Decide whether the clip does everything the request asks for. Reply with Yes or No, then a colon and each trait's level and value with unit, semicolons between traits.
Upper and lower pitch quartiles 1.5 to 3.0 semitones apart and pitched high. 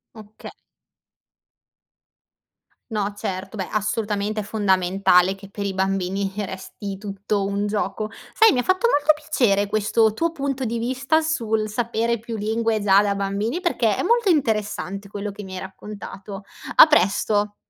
Yes: average, 2.7 semitones; high, 210 Hz